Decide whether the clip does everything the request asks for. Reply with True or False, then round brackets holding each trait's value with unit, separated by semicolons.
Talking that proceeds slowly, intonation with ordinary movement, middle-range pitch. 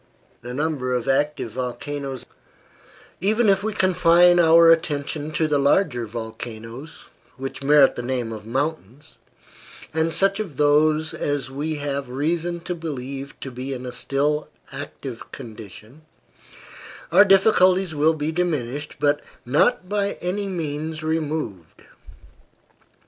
True (125 wpm; 4.1 semitones; 150 Hz)